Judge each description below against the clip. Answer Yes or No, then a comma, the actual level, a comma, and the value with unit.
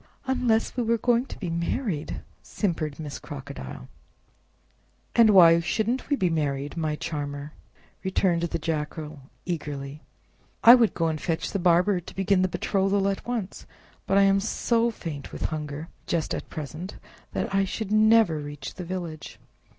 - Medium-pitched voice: Yes, medium, 175 Hz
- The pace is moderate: Yes, average, 160 wpm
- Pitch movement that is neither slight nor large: Yes, average, 4.9 semitones